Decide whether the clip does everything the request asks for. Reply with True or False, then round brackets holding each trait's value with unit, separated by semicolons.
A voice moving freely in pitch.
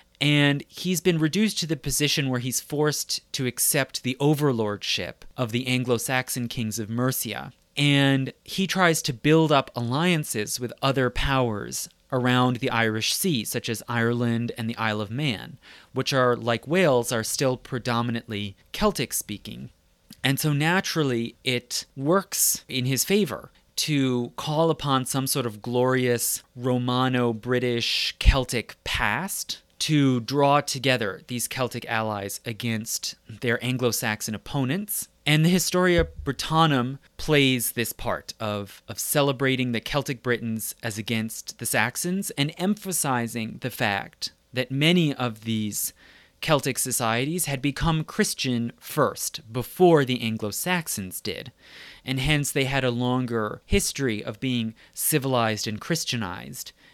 False (3.8 semitones)